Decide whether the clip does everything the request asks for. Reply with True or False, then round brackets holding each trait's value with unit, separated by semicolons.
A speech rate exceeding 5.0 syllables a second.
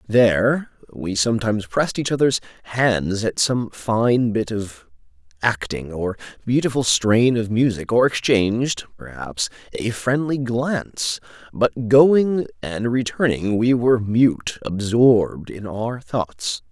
False (3.9 syllables/s)